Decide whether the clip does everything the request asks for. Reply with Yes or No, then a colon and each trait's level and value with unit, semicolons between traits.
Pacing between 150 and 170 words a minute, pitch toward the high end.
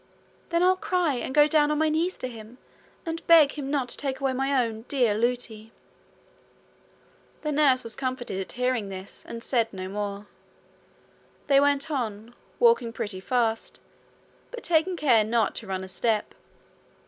Yes: average, 165 wpm; very high, 255 Hz